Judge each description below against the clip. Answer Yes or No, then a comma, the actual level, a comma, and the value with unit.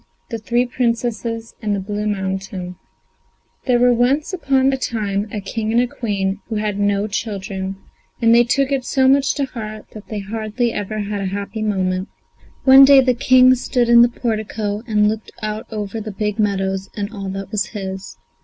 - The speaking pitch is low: No, high, 215 Hz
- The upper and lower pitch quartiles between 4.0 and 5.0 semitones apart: No, average, 3.2 semitones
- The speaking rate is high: No, average, 185 wpm